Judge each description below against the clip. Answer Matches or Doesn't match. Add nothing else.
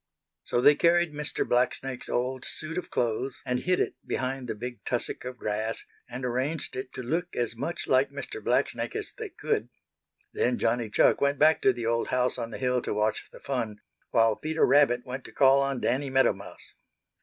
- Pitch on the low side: Matches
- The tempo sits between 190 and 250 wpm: Matches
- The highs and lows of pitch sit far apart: Doesn't match